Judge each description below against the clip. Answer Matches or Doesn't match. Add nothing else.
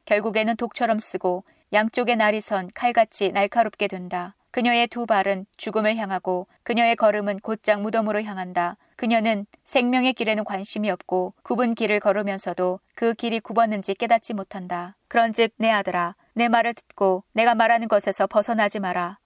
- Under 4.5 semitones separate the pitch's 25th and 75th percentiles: Matches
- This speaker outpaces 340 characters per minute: Matches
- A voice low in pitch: Doesn't match